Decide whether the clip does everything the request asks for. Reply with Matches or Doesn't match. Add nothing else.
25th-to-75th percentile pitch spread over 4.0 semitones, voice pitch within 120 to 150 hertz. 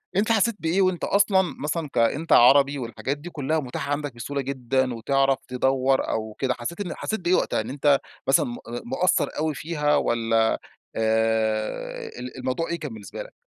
Matches